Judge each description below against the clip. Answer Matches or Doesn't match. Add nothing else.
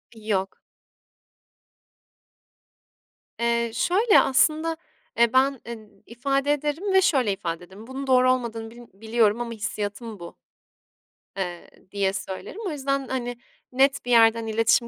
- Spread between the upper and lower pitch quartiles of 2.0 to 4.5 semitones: Matches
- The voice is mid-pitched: Doesn't match